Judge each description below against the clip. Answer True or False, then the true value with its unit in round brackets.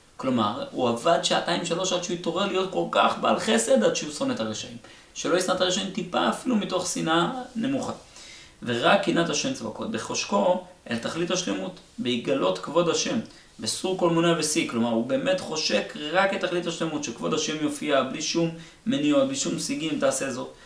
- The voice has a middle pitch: True (180 Hz)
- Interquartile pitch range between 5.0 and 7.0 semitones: False (4.3 semitones)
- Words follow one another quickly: True (175 wpm)